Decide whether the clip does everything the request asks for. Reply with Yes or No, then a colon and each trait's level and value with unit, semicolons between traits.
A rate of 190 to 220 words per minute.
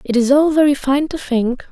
No: fast, 245 wpm